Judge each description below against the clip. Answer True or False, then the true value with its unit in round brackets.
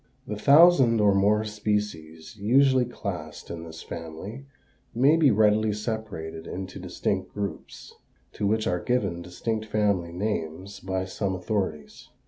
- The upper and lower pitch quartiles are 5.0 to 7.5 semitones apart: False (3.8 semitones)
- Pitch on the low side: True (105 Hz)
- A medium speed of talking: False (130 wpm)